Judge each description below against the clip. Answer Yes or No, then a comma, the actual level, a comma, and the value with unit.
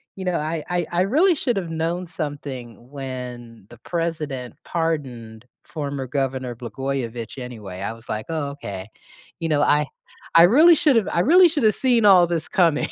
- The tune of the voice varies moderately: No, wide, 6.1 semitones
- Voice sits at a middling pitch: Yes, medium, 150 Hz